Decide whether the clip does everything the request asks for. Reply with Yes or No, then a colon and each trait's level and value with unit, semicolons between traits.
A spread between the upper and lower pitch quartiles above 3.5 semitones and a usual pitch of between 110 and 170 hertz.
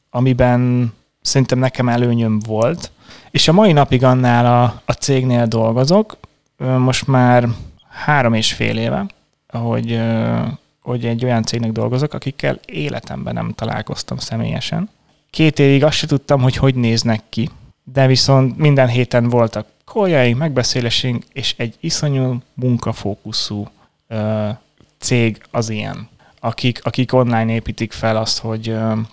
No: average, 2.8 semitones; low, 120 Hz